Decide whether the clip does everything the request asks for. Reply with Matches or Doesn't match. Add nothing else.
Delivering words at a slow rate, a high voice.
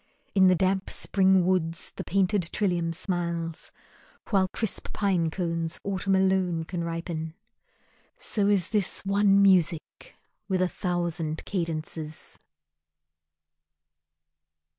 Doesn't match